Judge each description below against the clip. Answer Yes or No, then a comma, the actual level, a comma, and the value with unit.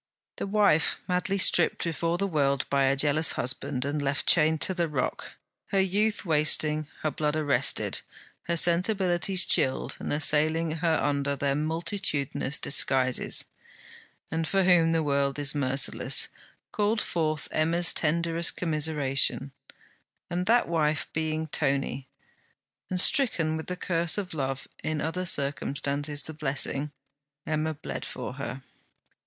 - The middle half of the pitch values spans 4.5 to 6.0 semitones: No, average, 3.2 semitones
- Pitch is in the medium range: Yes, medium, 155 Hz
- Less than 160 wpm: Yes, slow, 135 wpm